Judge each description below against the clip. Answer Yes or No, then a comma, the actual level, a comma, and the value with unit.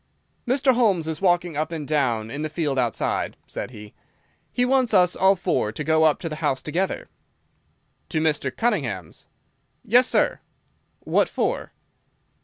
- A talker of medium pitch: Yes, medium, 160 Hz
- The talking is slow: No, average, 155 wpm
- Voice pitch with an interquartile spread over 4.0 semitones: Yes, wide, 5.4 semitones